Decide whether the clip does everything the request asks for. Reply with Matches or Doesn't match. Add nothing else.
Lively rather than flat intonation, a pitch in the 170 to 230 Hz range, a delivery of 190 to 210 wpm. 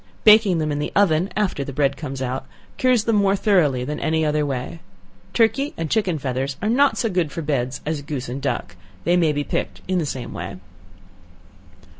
Doesn't match